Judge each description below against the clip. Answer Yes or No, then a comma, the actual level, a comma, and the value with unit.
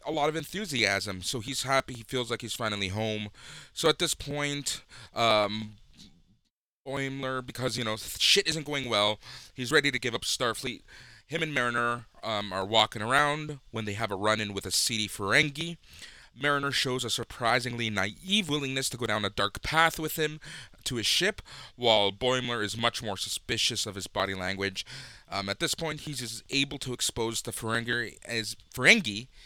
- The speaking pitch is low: Yes, low, 120 Hz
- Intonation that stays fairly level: No, average, 4.6 semitones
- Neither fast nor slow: Yes, average, 180 wpm